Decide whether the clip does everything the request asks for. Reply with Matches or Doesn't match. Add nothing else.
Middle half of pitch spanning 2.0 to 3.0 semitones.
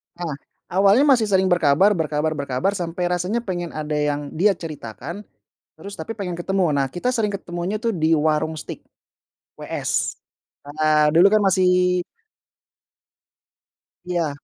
Doesn't match